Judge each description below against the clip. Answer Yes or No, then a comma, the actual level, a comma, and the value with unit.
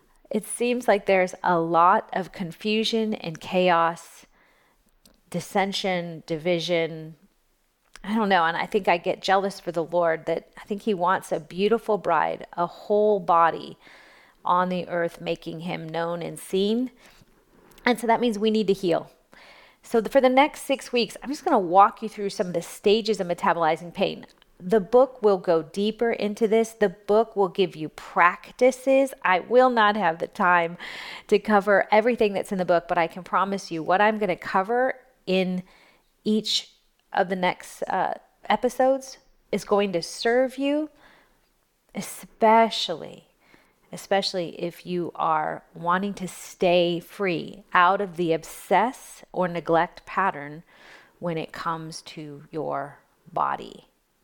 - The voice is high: Yes, high, 195 Hz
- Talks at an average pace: Yes, average, 155 wpm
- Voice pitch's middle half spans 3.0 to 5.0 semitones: Yes, average, 4.2 semitones